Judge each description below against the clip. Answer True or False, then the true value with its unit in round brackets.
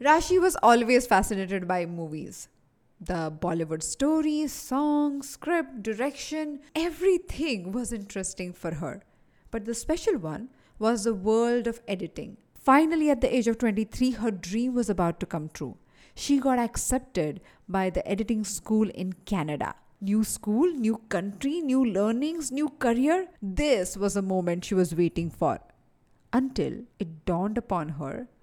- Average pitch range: False (6.4 semitones)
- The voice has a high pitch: True (225 Hz)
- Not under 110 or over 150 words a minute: True (145 wpm)